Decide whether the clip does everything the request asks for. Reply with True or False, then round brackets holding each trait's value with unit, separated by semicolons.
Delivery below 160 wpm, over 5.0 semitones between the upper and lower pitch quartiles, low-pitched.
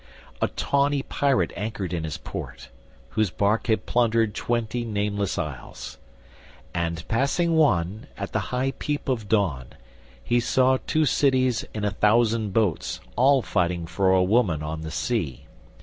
True (150 wpm; 5.6 semitones; 110 Hz)